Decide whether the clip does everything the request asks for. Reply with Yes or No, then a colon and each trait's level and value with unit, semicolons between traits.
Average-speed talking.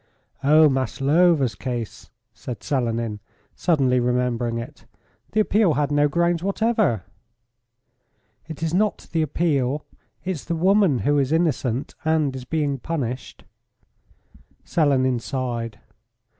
No: slow, 115 wpm